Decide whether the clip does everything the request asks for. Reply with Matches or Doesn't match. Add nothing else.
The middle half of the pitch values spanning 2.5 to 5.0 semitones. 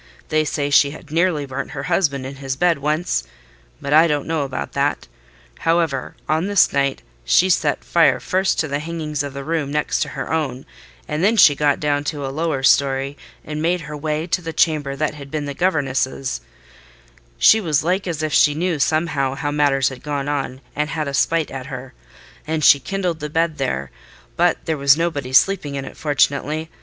Matches